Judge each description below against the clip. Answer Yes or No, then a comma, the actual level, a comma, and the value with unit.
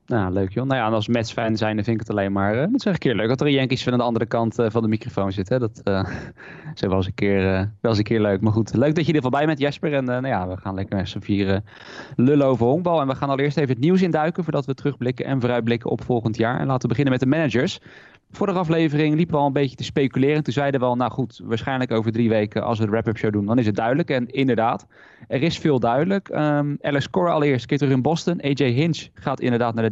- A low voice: Yes, low, 125 Hz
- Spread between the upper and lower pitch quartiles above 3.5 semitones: Yes, average, 4.3 semitones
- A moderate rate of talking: No, fast, 295 wpm